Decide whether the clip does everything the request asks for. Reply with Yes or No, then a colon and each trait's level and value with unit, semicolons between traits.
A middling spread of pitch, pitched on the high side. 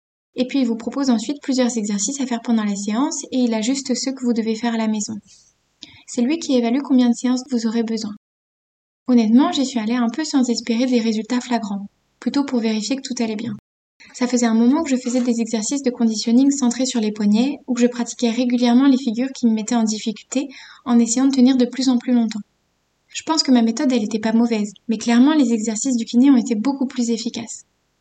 No: narrow, 2.2 semitones; high, 240 Hz